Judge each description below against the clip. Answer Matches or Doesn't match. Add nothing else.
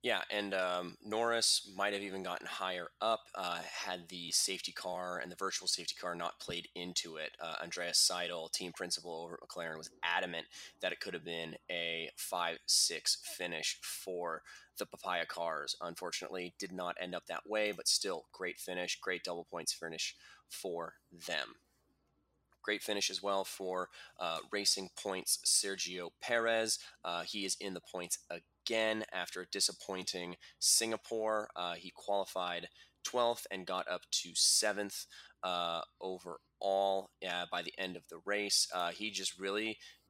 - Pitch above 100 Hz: Doesn't match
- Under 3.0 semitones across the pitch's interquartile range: Matches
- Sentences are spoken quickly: Doesn't match